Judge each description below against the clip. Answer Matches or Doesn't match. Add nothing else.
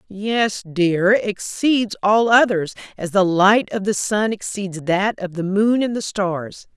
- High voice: Matches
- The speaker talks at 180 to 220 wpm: Doesn't match